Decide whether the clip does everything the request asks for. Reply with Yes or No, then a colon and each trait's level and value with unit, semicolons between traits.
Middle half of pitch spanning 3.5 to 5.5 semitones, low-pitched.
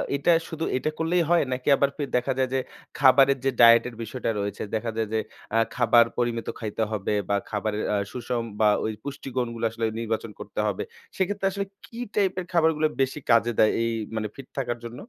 Yes: average, 3.9 semitones; low, 120 Hz